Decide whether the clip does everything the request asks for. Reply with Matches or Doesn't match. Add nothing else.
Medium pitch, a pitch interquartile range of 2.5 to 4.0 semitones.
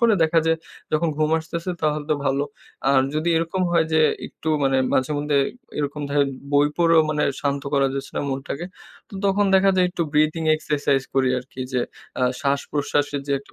Matches